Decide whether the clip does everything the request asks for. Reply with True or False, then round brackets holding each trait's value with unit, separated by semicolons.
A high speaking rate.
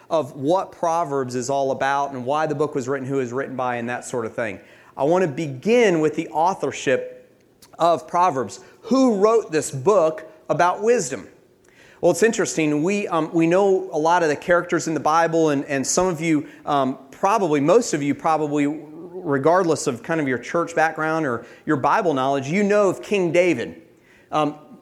False (195 wpm)